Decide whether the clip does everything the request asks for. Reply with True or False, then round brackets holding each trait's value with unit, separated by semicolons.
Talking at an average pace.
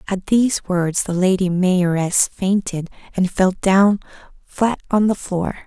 True (150 wpm)